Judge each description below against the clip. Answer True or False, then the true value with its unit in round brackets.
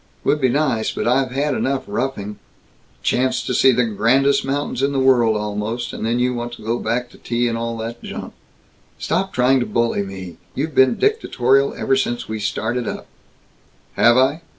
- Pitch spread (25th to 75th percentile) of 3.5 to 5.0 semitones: False (2.7 semitones)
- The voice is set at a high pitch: False (125 Hz)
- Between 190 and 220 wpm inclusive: True (200 wpm)